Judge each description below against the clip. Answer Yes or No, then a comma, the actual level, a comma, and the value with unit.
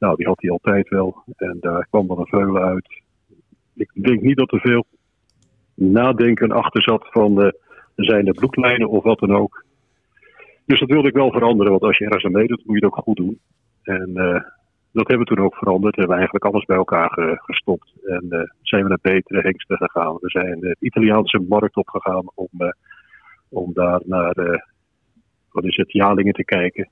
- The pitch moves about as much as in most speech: Yes, average, 3.3 semitones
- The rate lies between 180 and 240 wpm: Yes, average, 195 wpm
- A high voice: No, low, 100 Hz